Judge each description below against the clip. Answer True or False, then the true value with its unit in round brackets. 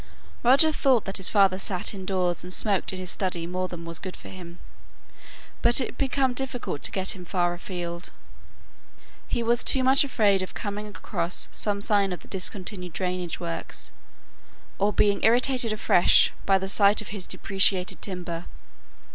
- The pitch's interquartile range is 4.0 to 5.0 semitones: False (3.0 semitones)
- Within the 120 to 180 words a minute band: True (170 wpm)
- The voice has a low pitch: False (195 Hz)